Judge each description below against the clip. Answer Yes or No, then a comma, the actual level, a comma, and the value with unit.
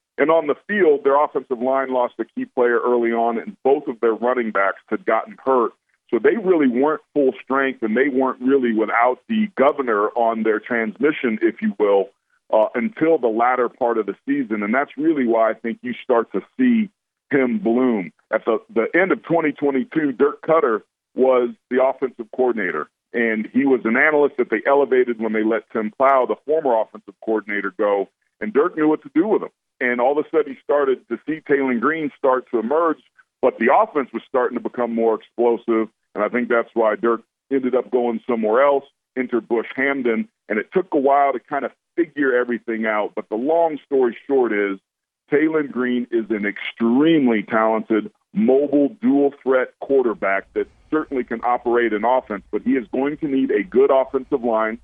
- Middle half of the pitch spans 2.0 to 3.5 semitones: No, average, 4.1 semitones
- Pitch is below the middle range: Yes, low, 125 Hz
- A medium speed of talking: Yes, average, 195 wpm